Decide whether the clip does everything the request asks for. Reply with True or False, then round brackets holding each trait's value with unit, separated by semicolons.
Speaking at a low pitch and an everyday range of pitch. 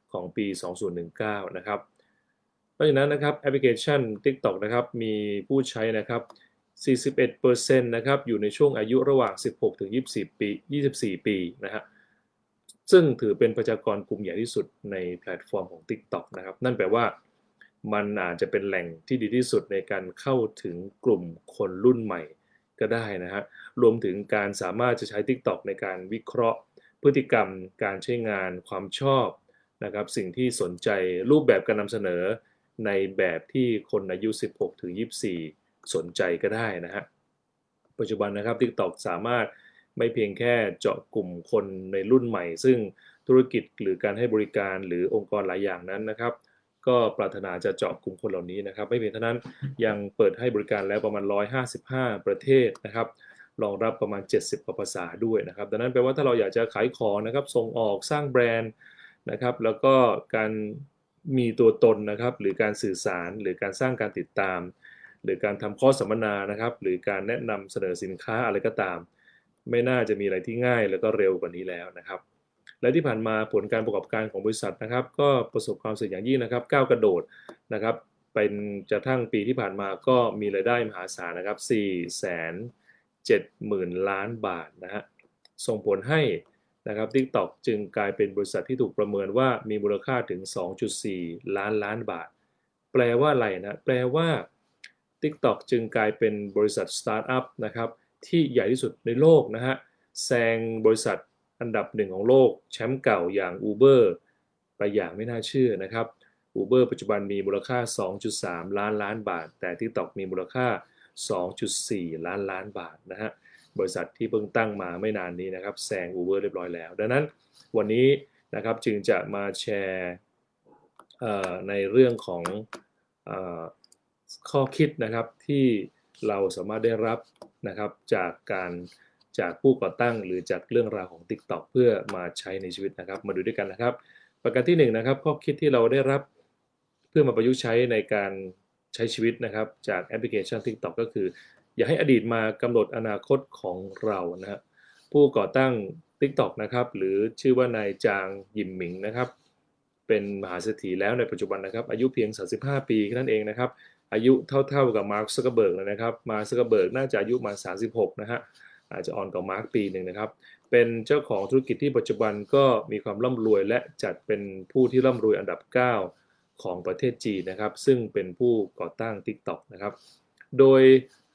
True (115 Hz; 4.4 semitones)